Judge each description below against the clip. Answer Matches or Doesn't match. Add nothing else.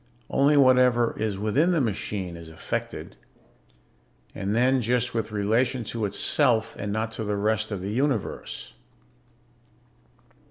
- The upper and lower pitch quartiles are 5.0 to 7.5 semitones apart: Doesn't match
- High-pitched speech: Doesn't match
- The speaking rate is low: Matches